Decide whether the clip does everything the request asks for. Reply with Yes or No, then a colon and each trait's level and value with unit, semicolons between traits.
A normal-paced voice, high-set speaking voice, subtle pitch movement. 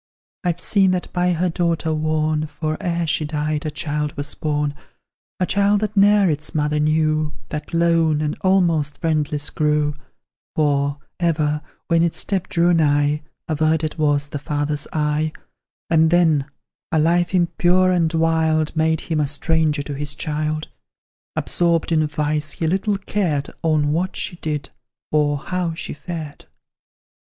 No: average, 150 wpm; medium, 155 Hz; narrow, 2.2 semitones